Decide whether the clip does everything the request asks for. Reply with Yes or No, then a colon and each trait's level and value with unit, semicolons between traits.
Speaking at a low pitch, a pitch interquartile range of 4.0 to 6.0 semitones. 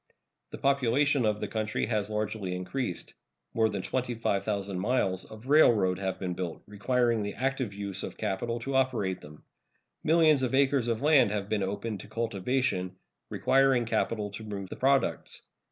Yes: low, 110 Hz; average, 4.7 semitones